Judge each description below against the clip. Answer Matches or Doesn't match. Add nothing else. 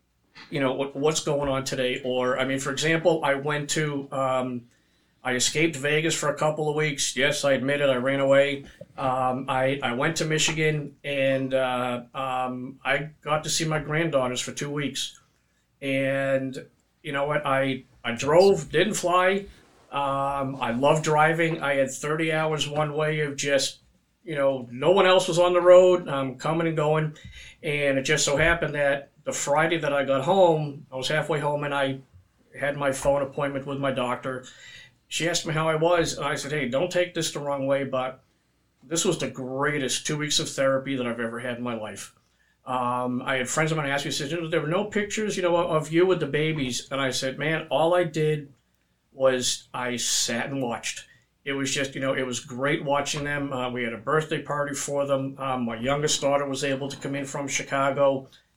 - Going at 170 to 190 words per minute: Doesn't match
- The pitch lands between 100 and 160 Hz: Matches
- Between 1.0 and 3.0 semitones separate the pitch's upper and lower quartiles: Matches